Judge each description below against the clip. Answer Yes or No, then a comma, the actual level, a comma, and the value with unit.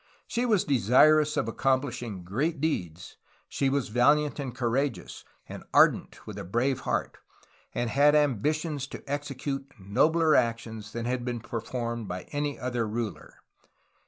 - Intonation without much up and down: No, average, 4.0 semitones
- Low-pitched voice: Yes, low, 130 Hz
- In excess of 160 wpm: No, average, 140 wpm